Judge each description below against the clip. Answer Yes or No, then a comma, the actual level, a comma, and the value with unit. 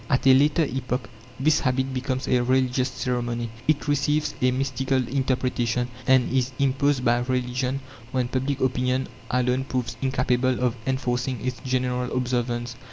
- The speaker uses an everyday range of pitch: No, narrow, 1.1 semitones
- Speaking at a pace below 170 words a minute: Yes, average, 145 wpm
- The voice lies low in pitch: Yes, low, 130 Hz